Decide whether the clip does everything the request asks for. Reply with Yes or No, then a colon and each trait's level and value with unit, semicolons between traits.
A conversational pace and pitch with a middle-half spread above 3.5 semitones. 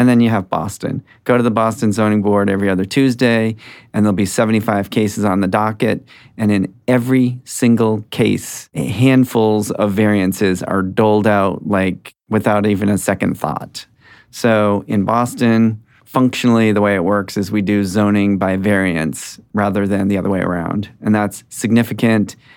No: average, 170 wpm; narrow, 2.5 semitones